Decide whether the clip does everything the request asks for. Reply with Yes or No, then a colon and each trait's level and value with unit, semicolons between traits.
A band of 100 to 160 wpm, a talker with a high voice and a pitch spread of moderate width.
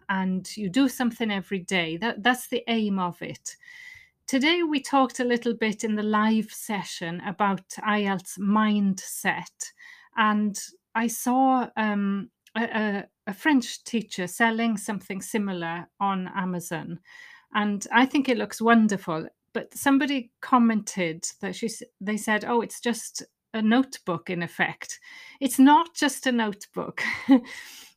Yes: slow, 135 wpm; high, 220 Hz; average, 4.6 semitones